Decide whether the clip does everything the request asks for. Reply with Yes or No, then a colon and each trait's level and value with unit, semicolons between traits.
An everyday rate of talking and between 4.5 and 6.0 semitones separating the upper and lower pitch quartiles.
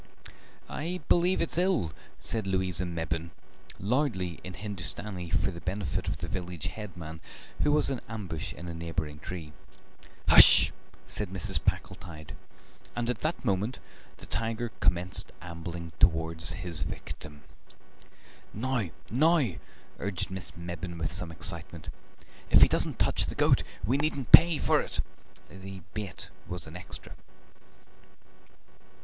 No: slow, 130 wpm; average, 5.0 semitones